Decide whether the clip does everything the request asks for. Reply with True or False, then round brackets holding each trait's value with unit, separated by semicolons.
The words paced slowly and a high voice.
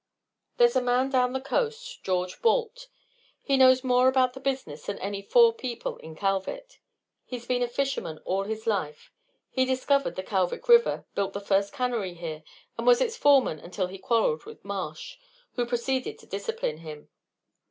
False (175 wpm; 245 Hz)